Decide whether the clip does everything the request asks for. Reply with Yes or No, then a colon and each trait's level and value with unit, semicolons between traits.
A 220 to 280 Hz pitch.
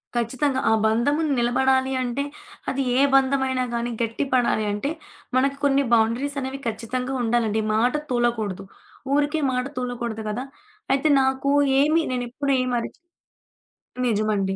Yes: very high, 250 Hz